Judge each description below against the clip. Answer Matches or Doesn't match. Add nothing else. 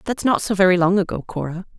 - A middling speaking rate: Doesn't match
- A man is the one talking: Doesn't match